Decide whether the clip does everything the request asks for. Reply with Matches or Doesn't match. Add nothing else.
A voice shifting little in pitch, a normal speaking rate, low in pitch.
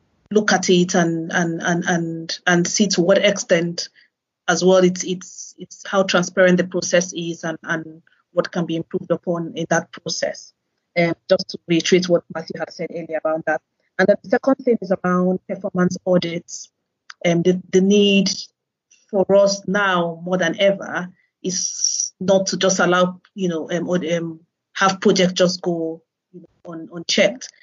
Doesn't match